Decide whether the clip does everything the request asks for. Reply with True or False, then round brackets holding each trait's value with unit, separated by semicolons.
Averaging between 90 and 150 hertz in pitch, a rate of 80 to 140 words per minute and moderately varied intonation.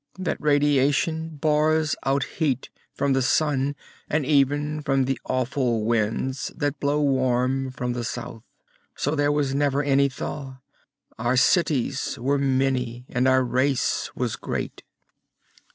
False (135 Hz; 135 wpm; 2.2 semitones)